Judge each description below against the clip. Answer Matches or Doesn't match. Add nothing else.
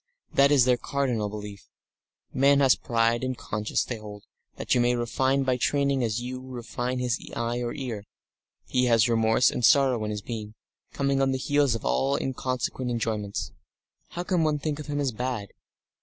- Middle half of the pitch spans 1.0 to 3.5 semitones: Matches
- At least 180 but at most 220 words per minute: Matches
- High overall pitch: Doesn't match